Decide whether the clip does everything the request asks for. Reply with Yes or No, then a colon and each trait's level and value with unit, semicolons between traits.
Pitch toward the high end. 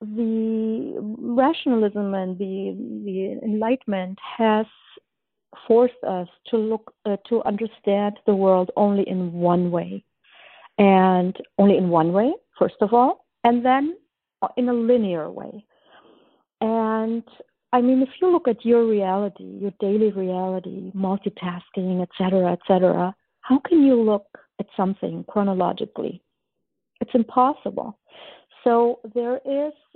Yes: high, 215 Hz